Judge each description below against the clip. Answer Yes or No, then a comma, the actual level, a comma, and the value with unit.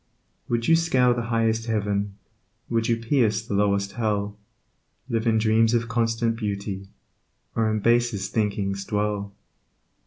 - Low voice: Yes, low, 110 Hz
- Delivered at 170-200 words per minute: No, slow, 135 wpm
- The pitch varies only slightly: Yes, narrow, 2.2 semitones